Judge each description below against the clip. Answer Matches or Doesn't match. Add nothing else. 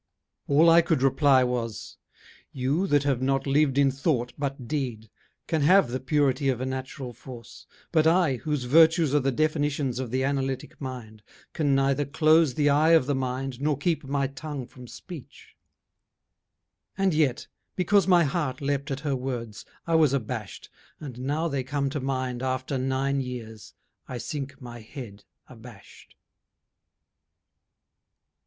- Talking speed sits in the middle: Matches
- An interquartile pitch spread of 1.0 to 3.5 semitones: Matches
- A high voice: Doesn't match